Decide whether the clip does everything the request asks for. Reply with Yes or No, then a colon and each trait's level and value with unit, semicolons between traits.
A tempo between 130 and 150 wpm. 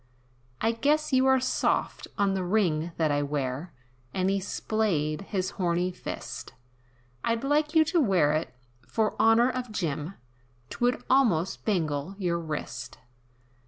Yes: average, 140 wpm